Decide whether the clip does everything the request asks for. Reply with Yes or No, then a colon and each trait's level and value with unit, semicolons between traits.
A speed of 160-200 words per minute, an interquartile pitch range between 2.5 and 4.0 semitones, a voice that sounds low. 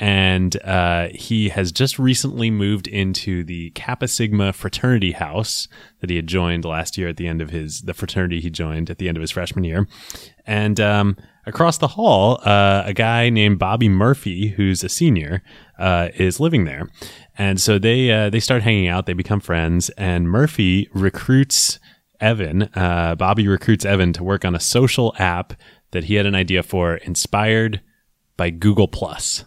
Yes: average, 180 wpm; average, 3.5 semitones; very low, 95 Hz